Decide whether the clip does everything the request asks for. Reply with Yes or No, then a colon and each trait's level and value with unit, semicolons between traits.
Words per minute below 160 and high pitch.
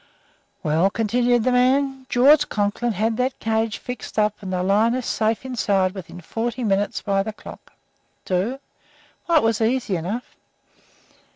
Yes: average, 150 wpm; high, 225 Hz